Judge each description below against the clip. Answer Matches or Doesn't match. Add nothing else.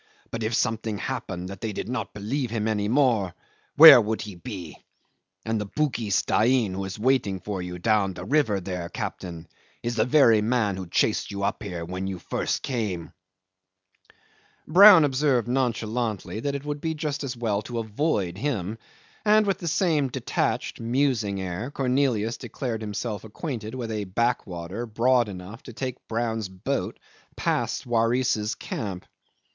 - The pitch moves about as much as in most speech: Matches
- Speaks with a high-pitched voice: Doesn't match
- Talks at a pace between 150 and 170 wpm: Matches